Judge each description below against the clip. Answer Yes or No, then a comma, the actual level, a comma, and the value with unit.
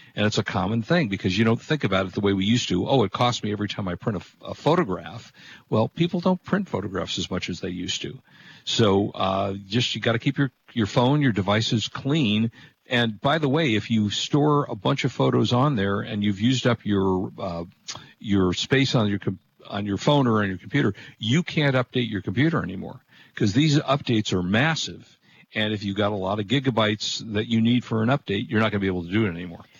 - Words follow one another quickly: Yes, fast, 240 wpm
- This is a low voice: Yes, low, 110 Hz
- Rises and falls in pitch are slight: No, average, 5.0 semitones